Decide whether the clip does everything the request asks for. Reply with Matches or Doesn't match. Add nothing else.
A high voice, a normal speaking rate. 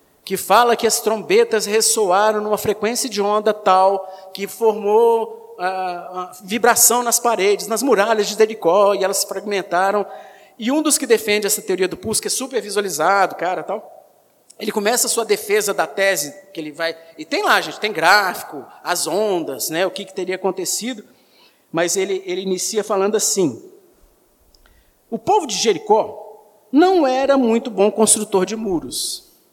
Matches